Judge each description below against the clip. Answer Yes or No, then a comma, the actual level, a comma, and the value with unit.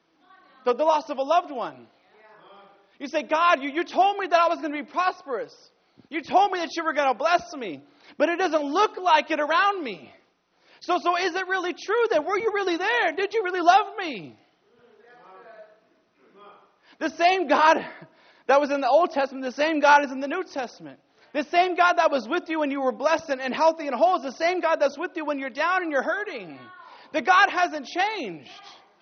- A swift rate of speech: Yes, fast, 215 wpm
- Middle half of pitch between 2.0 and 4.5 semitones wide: Yes, average, 4.1 semitones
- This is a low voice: No, very high, 330 Hz